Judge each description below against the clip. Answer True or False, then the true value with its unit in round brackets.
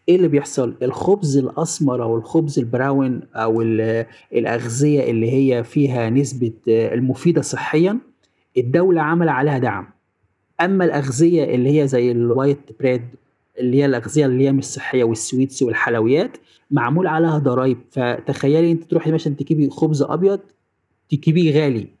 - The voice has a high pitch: False (135 Hz)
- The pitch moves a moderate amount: True (4.4 semitones)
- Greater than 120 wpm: True (130 wpm)